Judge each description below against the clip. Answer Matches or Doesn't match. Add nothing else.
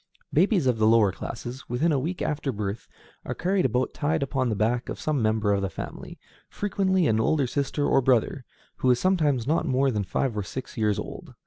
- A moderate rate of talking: Doesn't match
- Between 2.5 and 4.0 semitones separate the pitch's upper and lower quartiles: Doesn't match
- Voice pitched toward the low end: Matches